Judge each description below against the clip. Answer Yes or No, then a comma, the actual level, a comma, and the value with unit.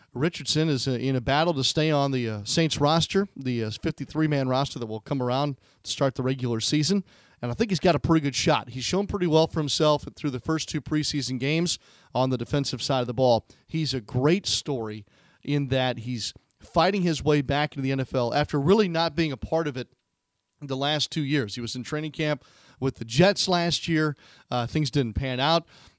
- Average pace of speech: No, fast, 215 wpm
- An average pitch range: Yes, average, 3.8 semitones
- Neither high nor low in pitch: Yes, medium, 145 Hz